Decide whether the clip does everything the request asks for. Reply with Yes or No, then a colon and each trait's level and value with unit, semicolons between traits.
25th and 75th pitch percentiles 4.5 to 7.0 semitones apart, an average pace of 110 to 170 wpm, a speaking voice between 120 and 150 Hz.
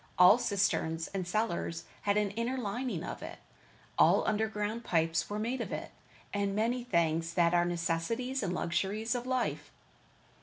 No: average, 5.1 semitones; average, 160 wpm; high, 205 Hz